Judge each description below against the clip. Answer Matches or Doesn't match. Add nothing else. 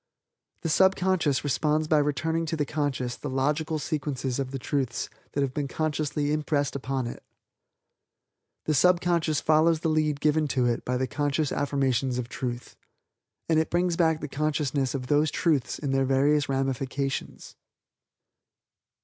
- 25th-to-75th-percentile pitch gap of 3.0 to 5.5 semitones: Doesn't match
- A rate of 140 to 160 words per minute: Matches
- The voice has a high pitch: Doesn't match